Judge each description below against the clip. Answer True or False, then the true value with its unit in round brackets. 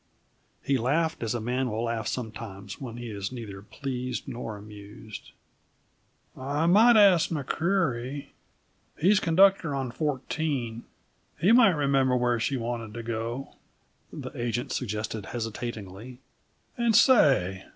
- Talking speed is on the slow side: True (125 wpm)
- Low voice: True (125 Hz)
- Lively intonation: False (4.8 semitones)